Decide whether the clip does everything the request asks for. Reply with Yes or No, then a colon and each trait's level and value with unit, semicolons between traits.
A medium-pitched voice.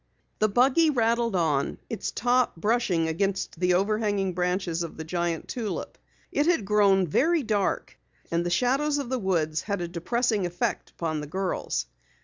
No: high, 195 Hz